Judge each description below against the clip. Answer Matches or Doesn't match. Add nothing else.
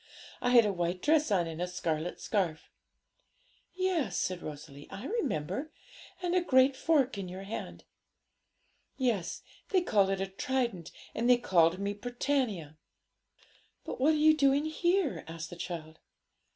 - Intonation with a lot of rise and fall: Matches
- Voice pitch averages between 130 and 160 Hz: Doesn't match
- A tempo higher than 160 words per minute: Doesn't match